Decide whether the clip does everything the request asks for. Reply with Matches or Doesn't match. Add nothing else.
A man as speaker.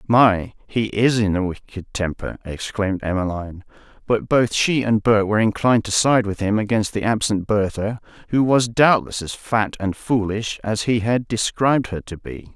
Matches